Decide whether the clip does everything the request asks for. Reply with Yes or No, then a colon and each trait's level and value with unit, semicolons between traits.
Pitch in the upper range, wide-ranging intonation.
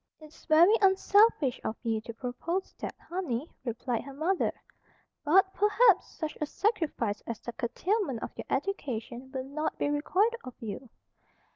Yes: very high, 295 Hz; wide, 7.6 semitones